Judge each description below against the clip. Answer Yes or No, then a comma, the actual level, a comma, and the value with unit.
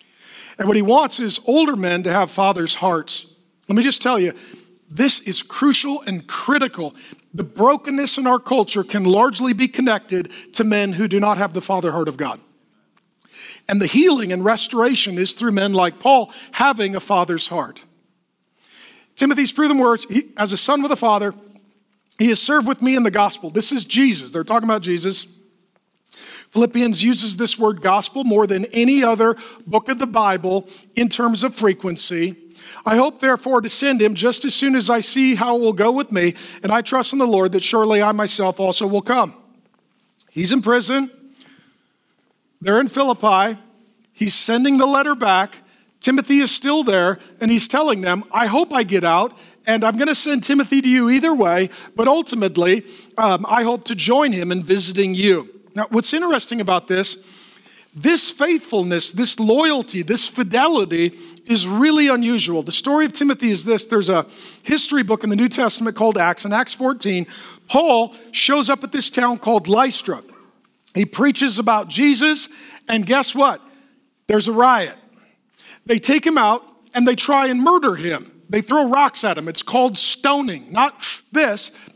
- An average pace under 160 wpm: No, average, 180 wpm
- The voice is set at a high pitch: Yes, high, 230 Hz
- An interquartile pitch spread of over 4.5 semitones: Yes, average, 5.2 semitones